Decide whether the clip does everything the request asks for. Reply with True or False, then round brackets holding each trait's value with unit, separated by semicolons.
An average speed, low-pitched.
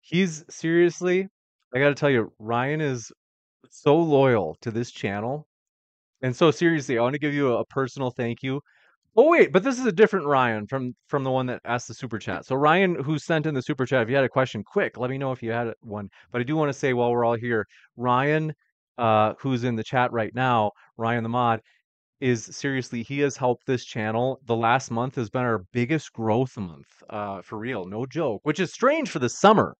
False (225 wpm; 130 Hz)